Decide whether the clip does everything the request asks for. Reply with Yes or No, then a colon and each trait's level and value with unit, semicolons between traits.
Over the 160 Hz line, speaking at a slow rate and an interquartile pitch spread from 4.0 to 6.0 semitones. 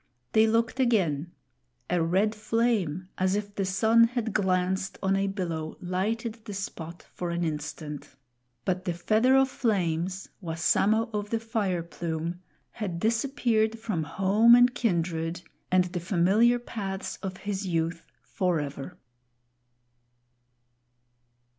Yes: high, 190 Hz; slow, 125 wpm; average, 4.4 semitones